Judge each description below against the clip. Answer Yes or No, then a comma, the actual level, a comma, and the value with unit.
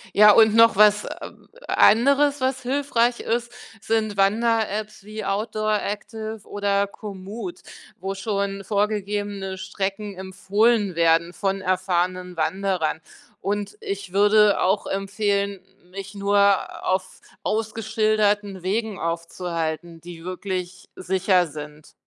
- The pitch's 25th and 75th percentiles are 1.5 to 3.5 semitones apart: Yes, narrow, 2.5 semitones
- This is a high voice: Yes, high, 200 Hz